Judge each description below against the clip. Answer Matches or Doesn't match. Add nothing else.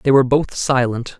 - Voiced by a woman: Doesn't match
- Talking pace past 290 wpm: Doesn't match